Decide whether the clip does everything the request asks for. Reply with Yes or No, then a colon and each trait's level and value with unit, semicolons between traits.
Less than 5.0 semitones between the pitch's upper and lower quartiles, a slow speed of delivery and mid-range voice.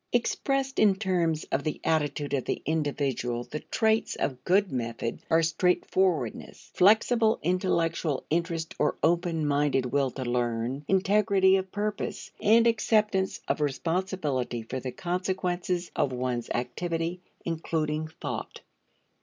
No: wide, 5.5 semitones; slow, 125 wpm; medium, 165 Hz